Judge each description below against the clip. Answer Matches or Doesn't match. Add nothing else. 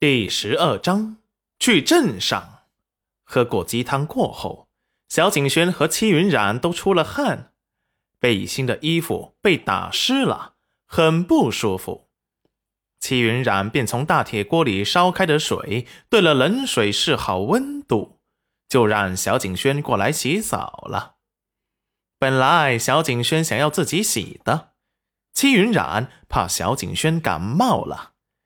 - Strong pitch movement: Matches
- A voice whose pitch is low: Doesn't match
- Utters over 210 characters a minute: Doesn't match